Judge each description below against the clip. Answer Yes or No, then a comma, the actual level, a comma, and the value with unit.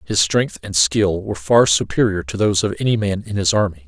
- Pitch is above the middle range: No, very low, 95 Hz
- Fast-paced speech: Yes, fast, 230 wpm